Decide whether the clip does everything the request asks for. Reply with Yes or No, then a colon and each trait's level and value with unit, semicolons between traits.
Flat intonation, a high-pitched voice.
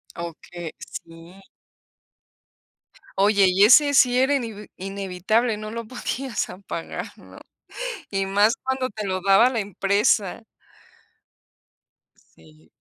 No: average, 3.8 semitones; high, 200 Hz